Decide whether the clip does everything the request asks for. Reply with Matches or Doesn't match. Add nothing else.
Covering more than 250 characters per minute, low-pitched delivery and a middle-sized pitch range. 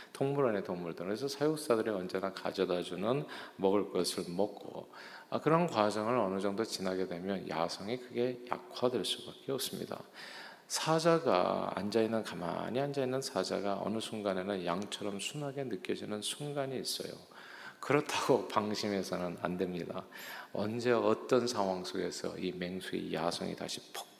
Matches